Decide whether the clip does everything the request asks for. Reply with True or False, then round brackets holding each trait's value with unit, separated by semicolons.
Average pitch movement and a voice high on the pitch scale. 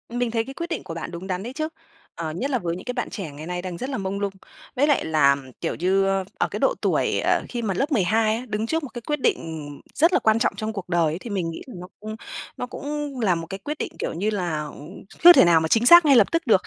False (6.6 semitones; 215 Hz)